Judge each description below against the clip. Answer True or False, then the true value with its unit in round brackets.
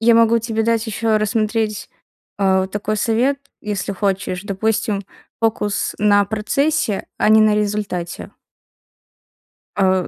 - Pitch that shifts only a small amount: True (2.0 semitones)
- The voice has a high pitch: True (210 Hz)